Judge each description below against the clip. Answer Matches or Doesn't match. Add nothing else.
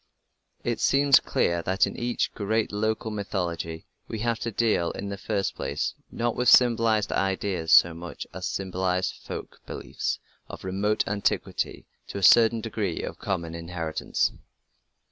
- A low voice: Matches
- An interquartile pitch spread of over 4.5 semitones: Doesn't match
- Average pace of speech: Matches